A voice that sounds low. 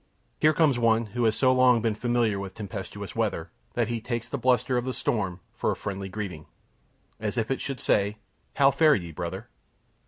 Yes: low, 115 Hz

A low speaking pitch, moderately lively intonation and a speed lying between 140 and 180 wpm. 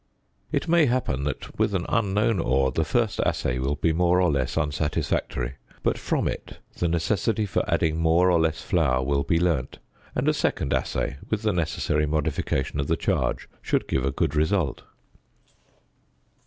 Yes: very low, 80 Hz; average, 4.5 semitones; average, 170 wpm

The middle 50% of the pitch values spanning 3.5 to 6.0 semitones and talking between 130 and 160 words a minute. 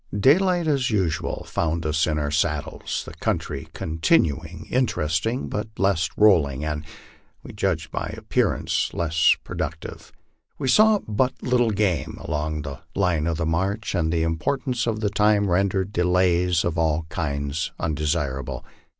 Yes: average, 5.3 semitones; average, 140 wpm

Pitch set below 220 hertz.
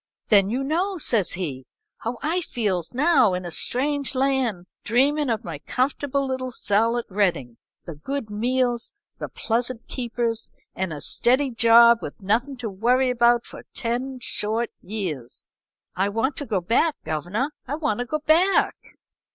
No: high, 235 Hz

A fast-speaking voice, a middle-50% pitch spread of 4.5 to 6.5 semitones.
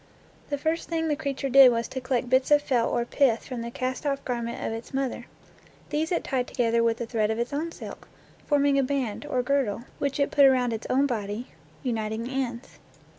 No: fast, 220 wpm; average, 3.2 semitones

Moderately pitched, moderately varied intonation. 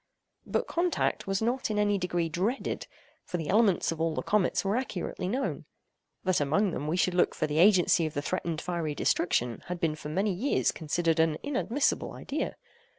Yes: medium, 180 Hz; average, 4.5 semitones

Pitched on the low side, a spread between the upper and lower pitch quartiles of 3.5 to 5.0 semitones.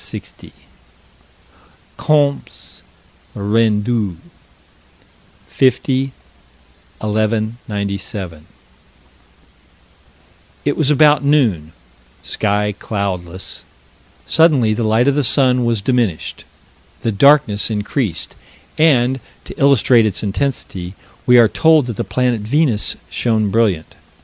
Yes: low, 115 Hz; average, 4.6 semitones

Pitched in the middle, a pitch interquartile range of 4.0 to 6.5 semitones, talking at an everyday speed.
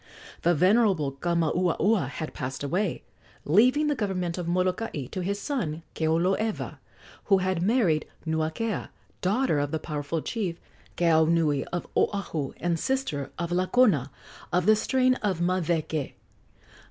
No: medium, 175 Hz; average, 4.4 semitones; slow, 130 wpm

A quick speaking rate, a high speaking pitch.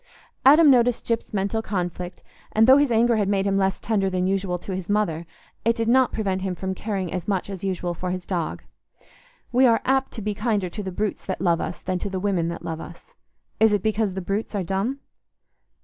Yes: fast, 225 wpm; high, 195 Hz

